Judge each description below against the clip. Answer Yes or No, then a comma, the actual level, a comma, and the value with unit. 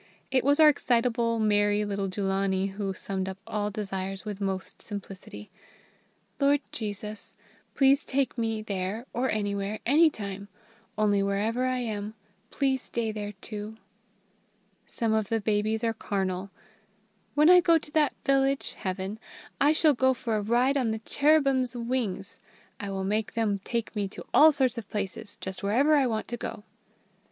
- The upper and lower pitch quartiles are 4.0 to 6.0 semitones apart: Yes, average, 4.3 semitones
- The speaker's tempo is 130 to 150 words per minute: No, average, 160 wpm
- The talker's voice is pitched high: Yes, high, 220 Hz